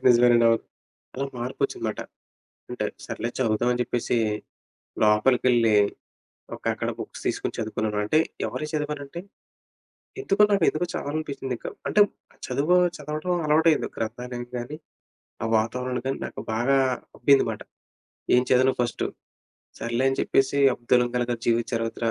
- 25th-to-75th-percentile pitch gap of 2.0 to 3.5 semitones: Yes, average, 3.2 semitones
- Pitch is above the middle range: No, low, 125 Hz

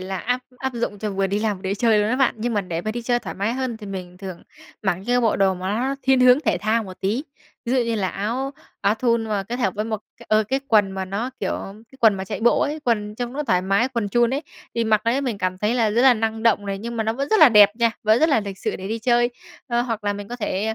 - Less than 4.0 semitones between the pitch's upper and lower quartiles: Yes, average, 3.3 semitones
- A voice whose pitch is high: Yes, high, 220 Hz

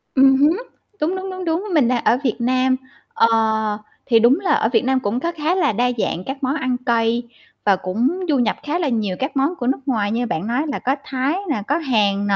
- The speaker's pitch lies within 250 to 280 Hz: Yes, very high, 255 Hz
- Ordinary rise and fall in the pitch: Yes, average, 4.4 semitones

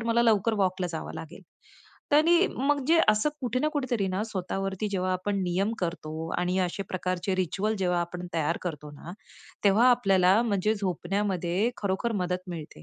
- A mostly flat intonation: No, average, 3.5 semitones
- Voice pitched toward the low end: No, high, 190 Hz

